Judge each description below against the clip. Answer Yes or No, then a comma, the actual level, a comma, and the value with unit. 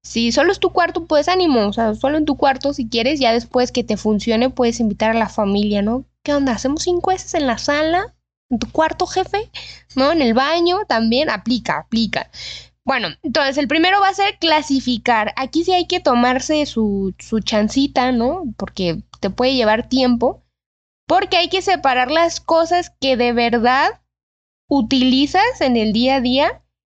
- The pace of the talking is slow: No, average, 185 wpm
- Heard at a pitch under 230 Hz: No, very high, 260 Hz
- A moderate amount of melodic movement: No, wide, 5.8 semitones